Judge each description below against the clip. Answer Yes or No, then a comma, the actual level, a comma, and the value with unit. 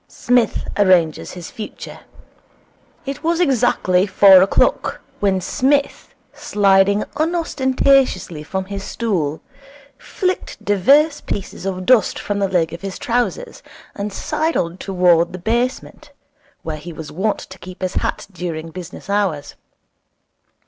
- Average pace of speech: No, slow, 125 wpm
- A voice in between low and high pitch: No, high, 195 Hz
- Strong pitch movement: Yes, wide, 5.7 semitones